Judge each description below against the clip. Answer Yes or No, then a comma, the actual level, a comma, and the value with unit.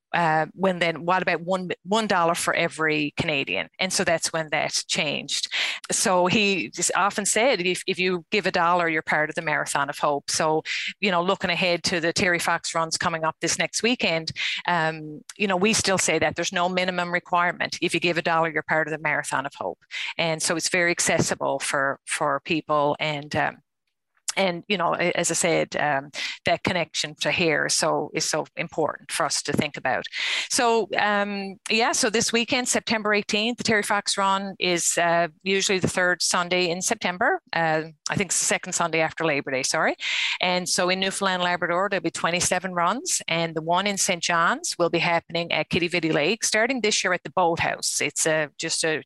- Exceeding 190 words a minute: Yes, fast, 205 wpm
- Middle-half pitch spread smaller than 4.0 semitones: Yes, average, 3.1 semitones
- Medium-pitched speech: Yes, medium, 175 Hz